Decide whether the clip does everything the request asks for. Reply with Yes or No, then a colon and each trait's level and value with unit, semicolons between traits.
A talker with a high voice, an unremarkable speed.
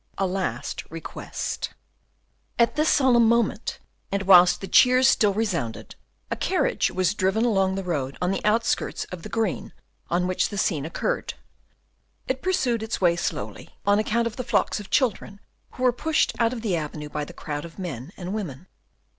Yes: high, 195 Hz; average, 180 wpm